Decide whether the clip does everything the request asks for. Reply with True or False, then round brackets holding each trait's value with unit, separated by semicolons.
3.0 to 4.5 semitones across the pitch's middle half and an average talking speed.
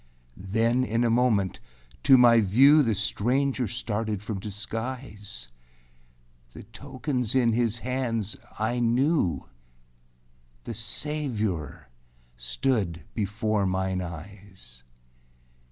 False (3.9 semitones; 105 wpm)